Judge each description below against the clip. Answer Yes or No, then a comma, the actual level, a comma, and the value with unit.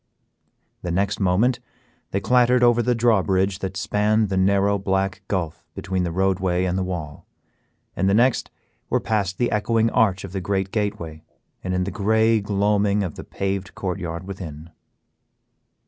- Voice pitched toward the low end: Yes, very low, 95 Hz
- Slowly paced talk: No, average, 165 wpm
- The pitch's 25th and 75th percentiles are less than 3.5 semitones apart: Yes, narrow, 2.4 semitones